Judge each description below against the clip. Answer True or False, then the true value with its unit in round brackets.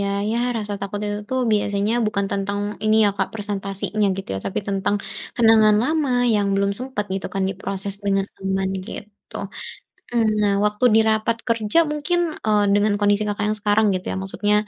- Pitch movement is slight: True (1.6 semitones)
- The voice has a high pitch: True (205 Hz)